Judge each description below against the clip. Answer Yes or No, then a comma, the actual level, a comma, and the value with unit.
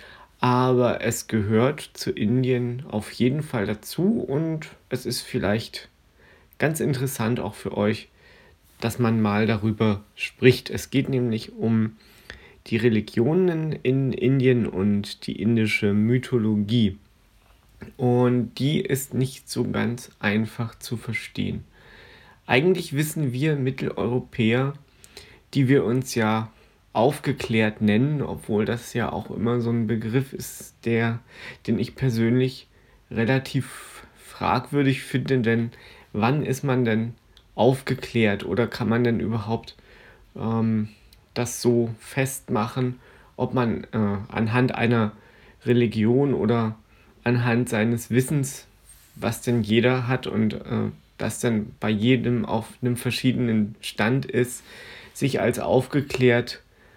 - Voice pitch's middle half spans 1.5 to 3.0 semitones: Yes, average, 2.7 semitones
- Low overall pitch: Yes, low, 120 Hz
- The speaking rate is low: Yes, slow, 120 wpm